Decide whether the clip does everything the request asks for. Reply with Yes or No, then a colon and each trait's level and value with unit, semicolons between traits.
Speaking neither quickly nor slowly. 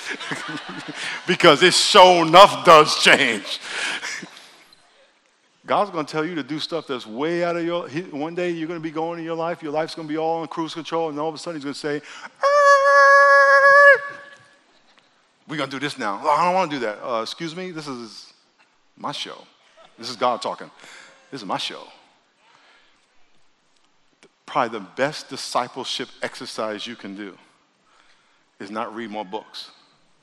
Yes: average, 160 wpm